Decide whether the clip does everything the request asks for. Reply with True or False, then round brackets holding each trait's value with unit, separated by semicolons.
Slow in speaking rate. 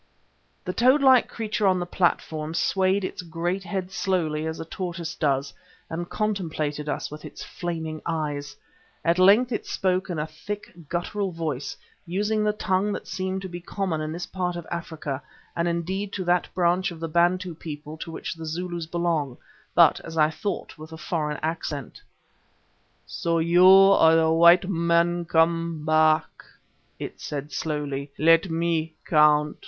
False (165 wpm)